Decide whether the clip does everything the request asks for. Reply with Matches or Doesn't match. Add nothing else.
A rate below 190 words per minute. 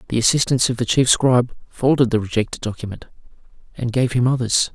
Matches